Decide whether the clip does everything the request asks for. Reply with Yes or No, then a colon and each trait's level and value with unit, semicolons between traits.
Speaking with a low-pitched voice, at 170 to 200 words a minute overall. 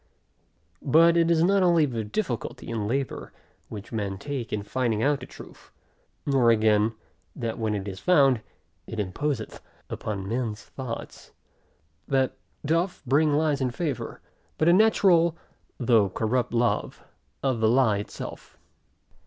No: low, 125 Hz; average, 140 wpm